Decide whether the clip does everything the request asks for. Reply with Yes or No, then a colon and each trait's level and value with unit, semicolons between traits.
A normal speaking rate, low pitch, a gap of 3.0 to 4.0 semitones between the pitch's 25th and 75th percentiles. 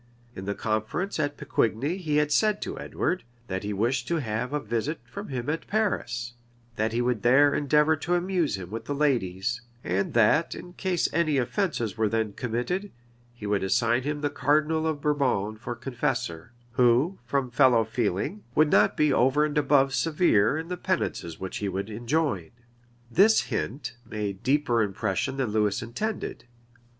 No: average, 170 wpm; low, 125 Hz; wide, 5.5 semitones